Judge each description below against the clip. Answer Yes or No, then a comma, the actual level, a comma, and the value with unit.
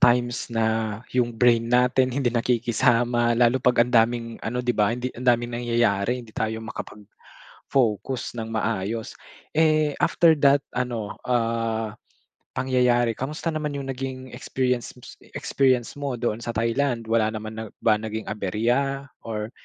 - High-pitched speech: No, low, 120 Hz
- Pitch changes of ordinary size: No, narrow, 2.1 semitones